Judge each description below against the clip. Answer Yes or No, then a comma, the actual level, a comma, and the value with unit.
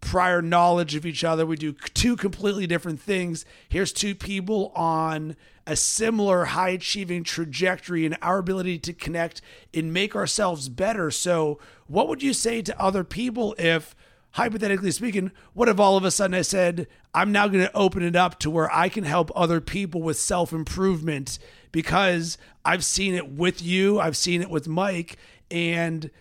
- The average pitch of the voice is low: No, medium, 180 Hz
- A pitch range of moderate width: Yes, average, 3.0 semitones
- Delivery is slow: No, average, 170 wpm